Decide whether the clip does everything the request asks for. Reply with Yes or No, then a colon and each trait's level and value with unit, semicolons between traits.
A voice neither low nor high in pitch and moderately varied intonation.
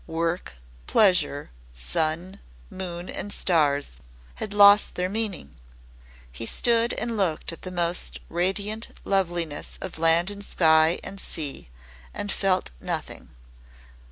Yes: medium, 180 Hz; average, 3.7 semitones